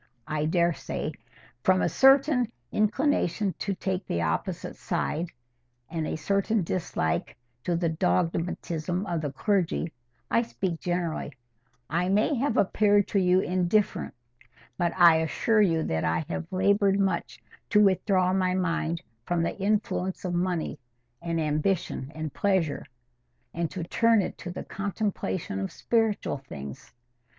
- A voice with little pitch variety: No, average, 4.0 semitones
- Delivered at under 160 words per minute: Yes, slow, 135 wpm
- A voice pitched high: No, medium, 180 Hz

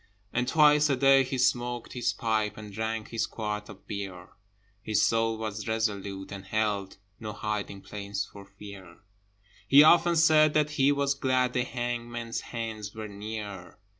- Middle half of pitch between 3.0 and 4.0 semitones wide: Yes, average, 3.7 semitones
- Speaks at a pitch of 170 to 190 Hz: No, low, 110 Hz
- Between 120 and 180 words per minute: Yes, average, 160 wpm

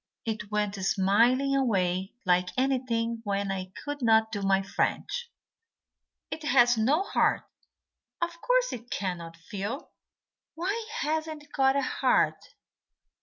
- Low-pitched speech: No, high, 235 Hz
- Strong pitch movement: Yes, wide, 6.7 semitones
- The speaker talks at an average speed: No, slow, 125 wpm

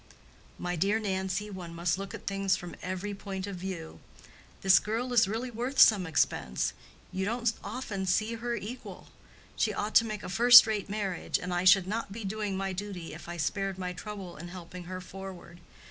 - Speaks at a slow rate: No, average, 190 wpm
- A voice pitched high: Yes, high, 195 Hz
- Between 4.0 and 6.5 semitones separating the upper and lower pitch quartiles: No, average, 2.9 semitones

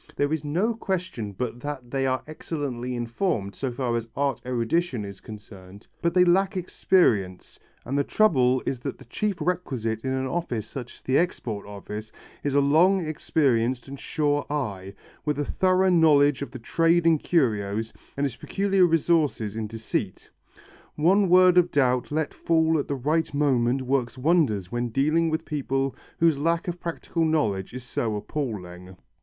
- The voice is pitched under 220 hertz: Yes, medium, 140 Hz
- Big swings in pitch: Yes, wide, 5.9 semitones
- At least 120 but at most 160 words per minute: No, average, 170 wpm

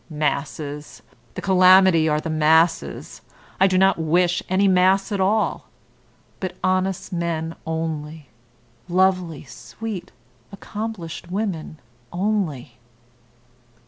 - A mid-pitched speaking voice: Yes, medium, 175 Hz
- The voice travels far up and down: No, average, 3.2 semitones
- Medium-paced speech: No, slow, 100 wpm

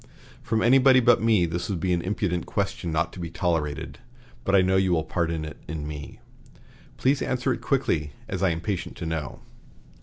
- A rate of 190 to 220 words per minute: Yes, average, 195 wpm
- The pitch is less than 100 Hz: Yes, very low, 90 Hz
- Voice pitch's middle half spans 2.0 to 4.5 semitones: No, average, 4.9 semitones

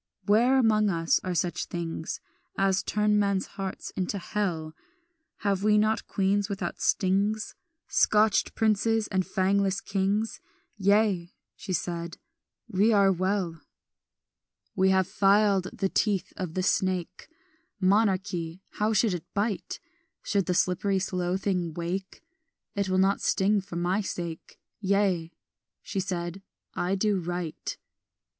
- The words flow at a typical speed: No, slow, 130 wpm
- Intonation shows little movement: Yes, narrow, 2.2 semitones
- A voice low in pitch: No, high, 195 Hz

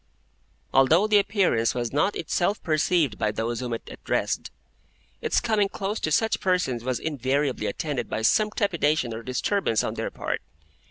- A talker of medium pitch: Yes, medium, 150 Hz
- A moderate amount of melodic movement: No, wide, 8.3 semitones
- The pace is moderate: Yes, average, 160 wpm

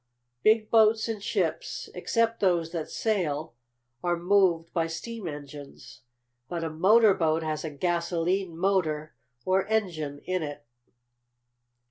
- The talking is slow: Yes, slow, 125 wpm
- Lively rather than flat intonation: No, average, 4.1 semitones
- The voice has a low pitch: No, medium, 175 Hz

